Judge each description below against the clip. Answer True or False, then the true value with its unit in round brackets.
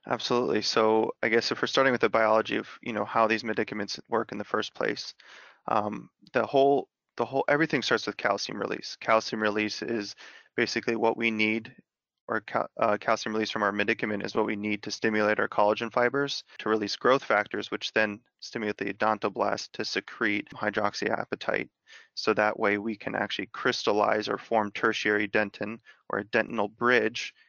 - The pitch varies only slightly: True (1.4 semitones)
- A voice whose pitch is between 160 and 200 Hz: False (110 Hz)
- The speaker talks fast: False (180 wpm)